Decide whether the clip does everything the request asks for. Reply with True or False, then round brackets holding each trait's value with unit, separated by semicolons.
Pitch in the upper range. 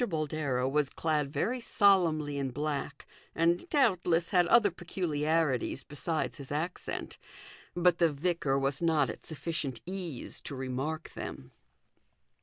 False (155 Hz)